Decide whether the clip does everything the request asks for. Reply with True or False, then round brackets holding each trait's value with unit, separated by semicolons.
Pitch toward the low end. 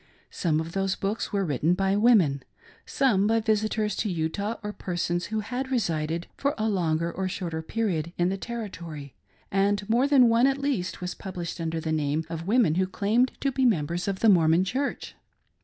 False (195 Hz)